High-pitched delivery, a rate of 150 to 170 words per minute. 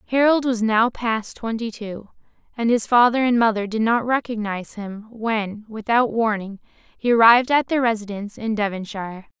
Yes: high, 225 Hz; average, 160 wpm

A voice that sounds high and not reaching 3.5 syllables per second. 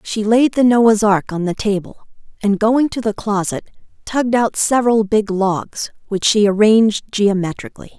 No: high, 210 Hz; 4.8 syllables/s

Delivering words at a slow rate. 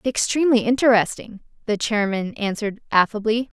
Yes: slow, 115 wpm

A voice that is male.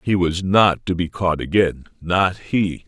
Yes: male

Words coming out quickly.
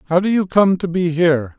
Yes: fast, 265 wpm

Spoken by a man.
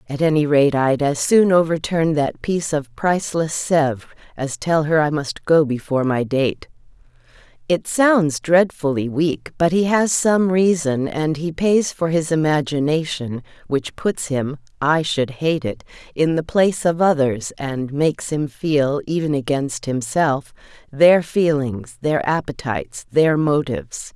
No: female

